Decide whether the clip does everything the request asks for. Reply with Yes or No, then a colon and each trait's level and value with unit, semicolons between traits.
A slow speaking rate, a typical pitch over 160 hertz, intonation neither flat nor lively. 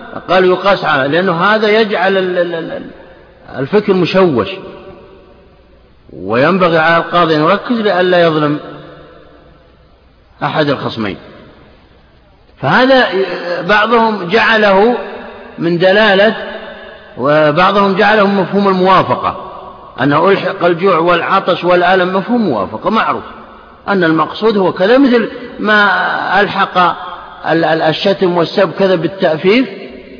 No: average, 90 wpm; high, 190 Hz; average, 3.1 semitones